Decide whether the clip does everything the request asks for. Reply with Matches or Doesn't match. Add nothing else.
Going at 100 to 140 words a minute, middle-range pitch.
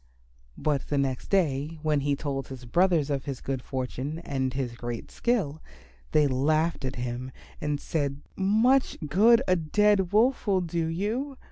Doesn't match